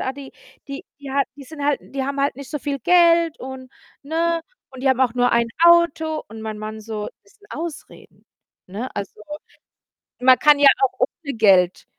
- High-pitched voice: Yes, very high, 275 Hz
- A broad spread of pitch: No, average, 4.3 semitones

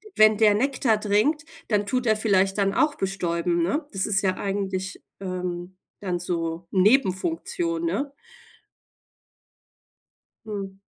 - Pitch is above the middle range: Yes, high, 200 Hz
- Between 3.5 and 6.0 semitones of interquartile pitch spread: No, average, 3.1 semitones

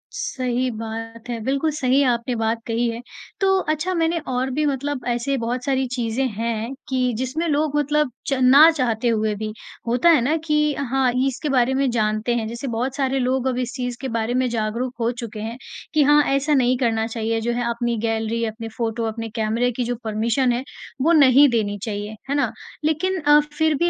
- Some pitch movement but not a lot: Yes, average, 3.3 semitones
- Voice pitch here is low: No, very high, 250 Hz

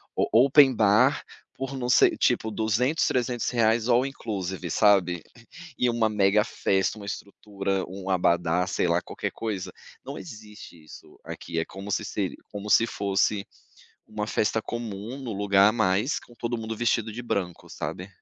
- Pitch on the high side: No, low, 105 Hz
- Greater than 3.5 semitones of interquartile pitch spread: No, average, 3.2 semitones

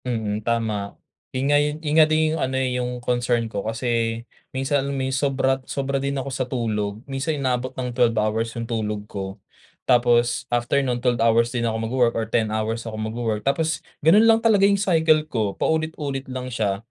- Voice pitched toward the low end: Yes, low, 125 Hz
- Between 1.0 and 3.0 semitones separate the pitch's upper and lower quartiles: No, average, 3.4 semitones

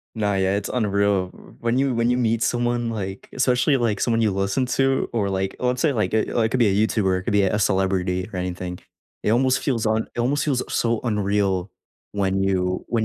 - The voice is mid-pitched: No, low, 110 Hz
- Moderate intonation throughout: Yes, average, 3.9 semitones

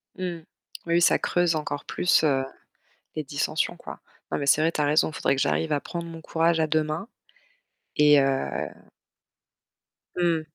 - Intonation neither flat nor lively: No, narrow, 2.2 semitones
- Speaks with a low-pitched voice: No, medium, 155 Hz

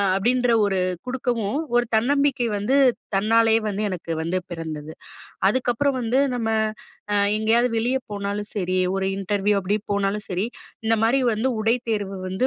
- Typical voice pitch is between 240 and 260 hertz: No, high, 215 Hz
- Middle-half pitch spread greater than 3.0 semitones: Yes, average, 3.7 semitones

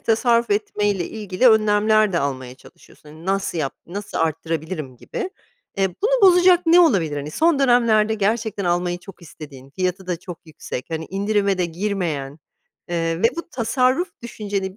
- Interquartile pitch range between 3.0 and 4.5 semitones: No, average, 5.2 semitones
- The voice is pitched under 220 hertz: Yes, high, 195 Hz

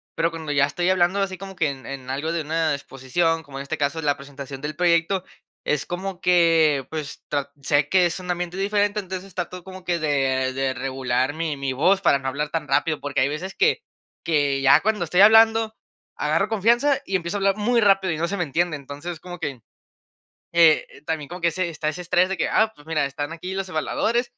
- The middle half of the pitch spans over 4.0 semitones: Yes, average, 4.6 semitones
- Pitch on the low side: No, medium, 165 Hz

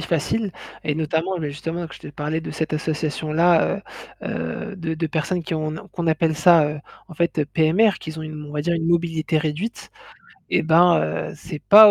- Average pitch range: No, narrow, 1.9 semitones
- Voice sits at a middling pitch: Yes, medium, 160 Hz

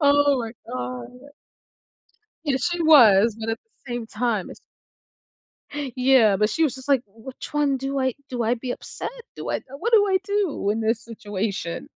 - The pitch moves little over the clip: No, average, 4.6 semitones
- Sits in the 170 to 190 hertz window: No, high, 245 Hz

